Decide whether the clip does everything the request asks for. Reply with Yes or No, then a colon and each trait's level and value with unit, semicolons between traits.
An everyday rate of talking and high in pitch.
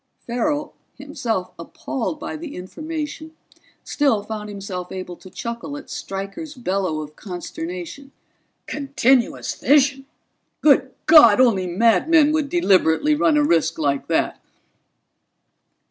No: slow, 115 wpm; high, 240 Hz